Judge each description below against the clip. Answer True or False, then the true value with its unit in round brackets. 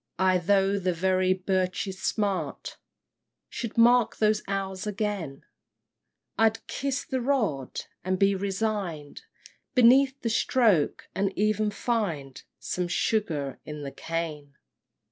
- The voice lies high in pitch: True (195 Hz)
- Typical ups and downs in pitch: True (3.7 semitones)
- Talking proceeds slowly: True (115 wpm)